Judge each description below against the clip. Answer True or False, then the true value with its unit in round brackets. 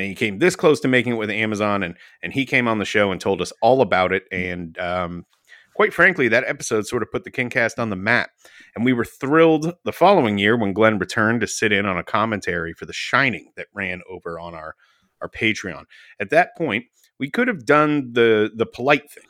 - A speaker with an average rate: False (235 wpm)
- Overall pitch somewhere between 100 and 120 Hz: True (110 Hz)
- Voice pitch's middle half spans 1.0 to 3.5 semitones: False (5.4 semitones)